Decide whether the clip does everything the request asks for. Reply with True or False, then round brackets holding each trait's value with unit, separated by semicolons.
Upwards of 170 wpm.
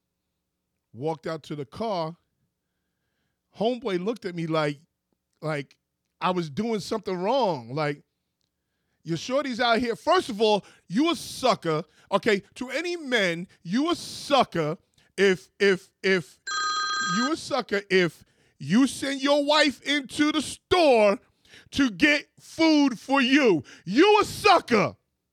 False (135 wpm)